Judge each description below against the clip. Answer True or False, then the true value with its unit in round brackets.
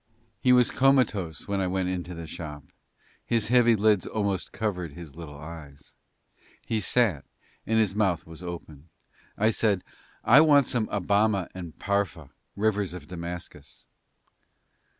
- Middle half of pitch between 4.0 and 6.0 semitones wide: True (4.4 semitones)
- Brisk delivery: False (145 wpm)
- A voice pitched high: False (95 Hz)